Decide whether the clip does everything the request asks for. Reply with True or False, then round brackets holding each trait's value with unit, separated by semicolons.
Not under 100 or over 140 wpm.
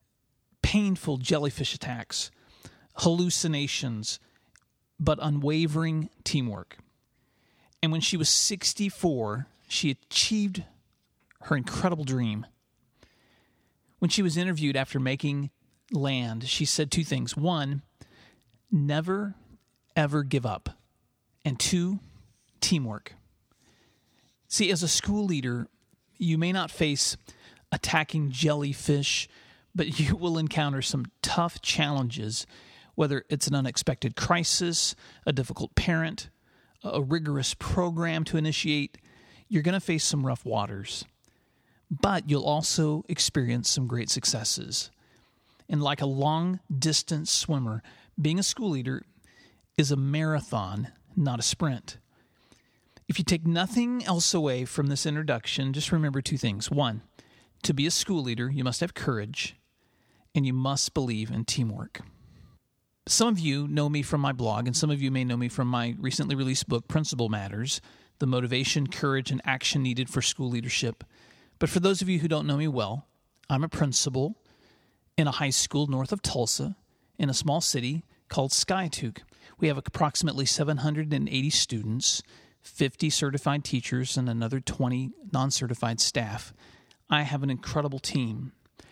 True (135 wpm)